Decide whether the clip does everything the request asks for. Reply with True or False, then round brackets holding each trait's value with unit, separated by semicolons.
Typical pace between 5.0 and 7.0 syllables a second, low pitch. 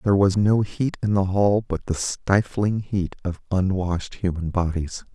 False (4.5 syllables/s; 95 Hz)